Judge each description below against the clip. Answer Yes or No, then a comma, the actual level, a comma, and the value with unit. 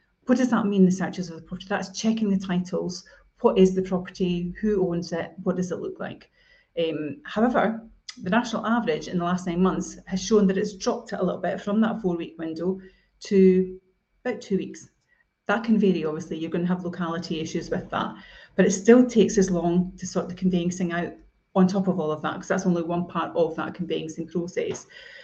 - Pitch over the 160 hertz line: Yes, medium, 185 Hz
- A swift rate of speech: Yes, fast, 215 wpm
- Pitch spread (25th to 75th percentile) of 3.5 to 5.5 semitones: No, average, 2.8 semitones